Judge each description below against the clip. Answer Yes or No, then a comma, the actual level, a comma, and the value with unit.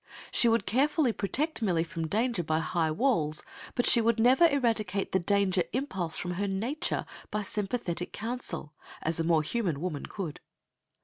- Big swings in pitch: Yes, wide, 6.0 semitones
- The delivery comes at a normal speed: Yes, average, 165 wpm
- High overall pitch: Yes, high, 200 Hz